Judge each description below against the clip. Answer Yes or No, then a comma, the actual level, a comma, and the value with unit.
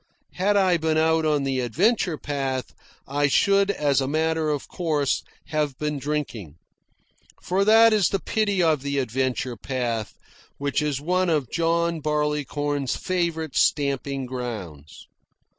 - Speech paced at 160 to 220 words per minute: No, average, 140 wpm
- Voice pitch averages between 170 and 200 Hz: No, medium, 150 Hz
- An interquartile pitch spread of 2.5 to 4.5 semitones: Yes, average, 4.0 semitones